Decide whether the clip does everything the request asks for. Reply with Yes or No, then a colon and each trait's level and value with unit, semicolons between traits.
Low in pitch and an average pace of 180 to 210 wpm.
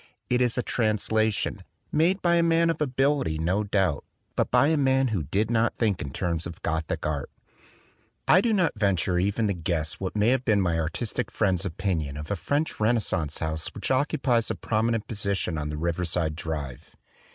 Yes: low, 100 Hz; average, 185 wpm